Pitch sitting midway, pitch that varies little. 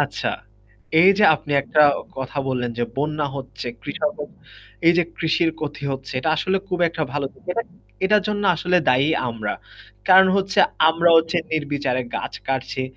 No: medium, 150 Hz; average, 5.1 semitones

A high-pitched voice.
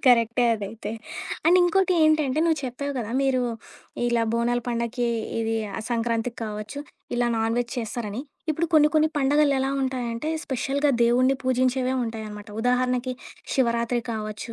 Yes: high, 245 Hz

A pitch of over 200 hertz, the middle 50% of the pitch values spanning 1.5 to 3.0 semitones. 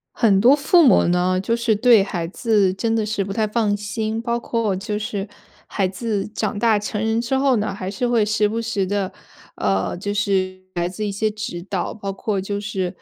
Yes: high, 210 Hz; narrow, 2.5 semitones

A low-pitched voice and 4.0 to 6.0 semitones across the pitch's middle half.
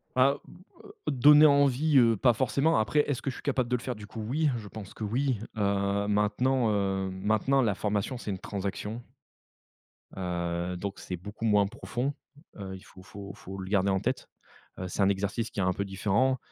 Yes: low, 105 Hz; average, 4.7 semitones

